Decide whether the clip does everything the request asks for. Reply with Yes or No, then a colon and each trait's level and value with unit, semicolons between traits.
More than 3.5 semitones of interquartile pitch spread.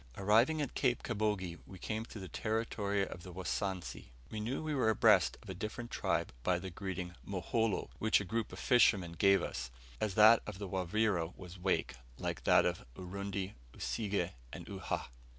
No: average, 3.1 semitones